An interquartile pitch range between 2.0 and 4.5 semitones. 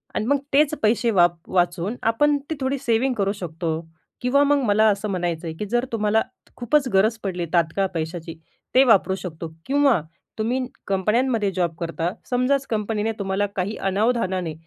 No: wide, 5.5 semitones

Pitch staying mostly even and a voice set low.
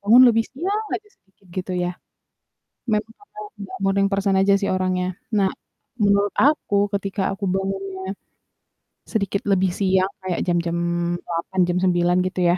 No: narrow, 1.5 semitones; high, 195 Hz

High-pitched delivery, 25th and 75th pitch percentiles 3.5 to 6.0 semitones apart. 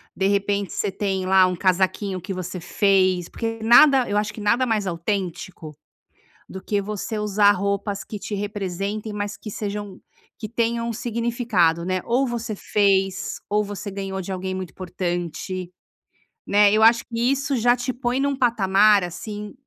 No: high, 205 Hz; average, 3.0 semitones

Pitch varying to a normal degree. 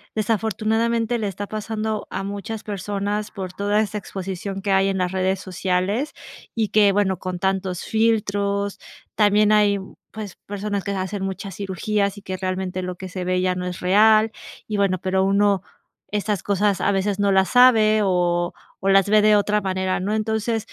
No: narrow, 2.0 semitones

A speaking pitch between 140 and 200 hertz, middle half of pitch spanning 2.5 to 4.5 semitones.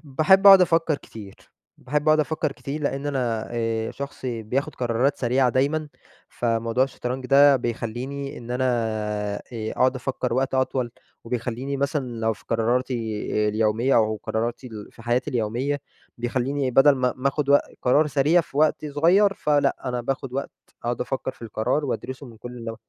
No: low, 130 Hz; average, 3.2 semitones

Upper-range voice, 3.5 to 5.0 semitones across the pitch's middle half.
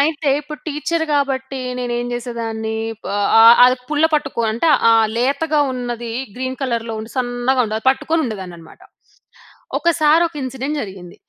Yes: very high, 255 Hz; average, 4.1 semitones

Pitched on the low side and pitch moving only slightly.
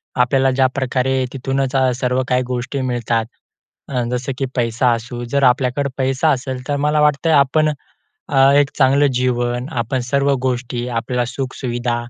Yes: low, 130 Hz; narrow, 1.9 semitones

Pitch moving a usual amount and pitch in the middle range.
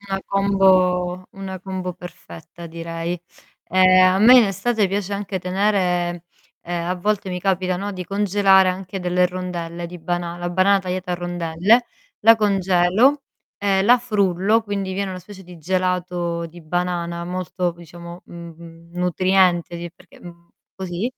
No: narrow, 1.9 semitones; medium, 180 Hz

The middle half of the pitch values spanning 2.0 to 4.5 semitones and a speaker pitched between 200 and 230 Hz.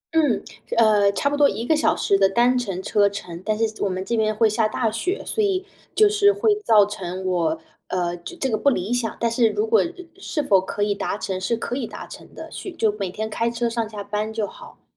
No: average, 5.0 semitones; high, 220 Hz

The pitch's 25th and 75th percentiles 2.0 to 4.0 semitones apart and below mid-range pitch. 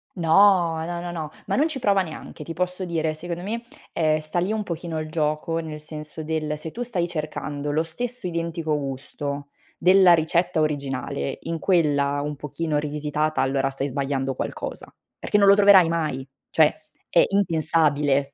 No: average, 2.8 semitones; medium, 160 Hz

